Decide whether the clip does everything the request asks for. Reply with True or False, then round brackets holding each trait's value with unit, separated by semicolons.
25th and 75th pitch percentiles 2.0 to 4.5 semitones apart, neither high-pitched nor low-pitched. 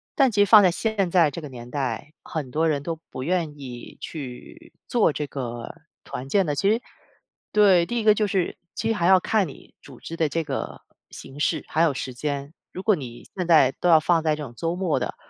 False (5.2 semitones; 160 Hz)